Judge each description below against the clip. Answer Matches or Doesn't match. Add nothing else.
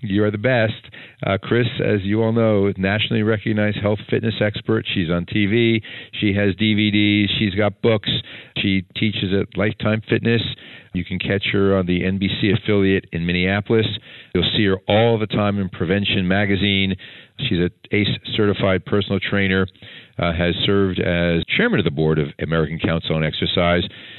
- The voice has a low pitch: Matches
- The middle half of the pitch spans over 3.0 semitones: Doesn't match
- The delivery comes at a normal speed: Matches